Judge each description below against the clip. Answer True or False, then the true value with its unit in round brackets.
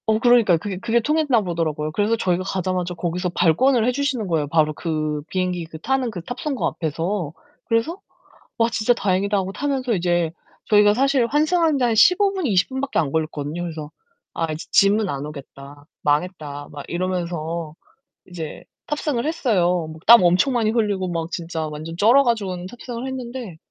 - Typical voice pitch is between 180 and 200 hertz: True (185 Hz)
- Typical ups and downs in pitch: False (6.5 semitones)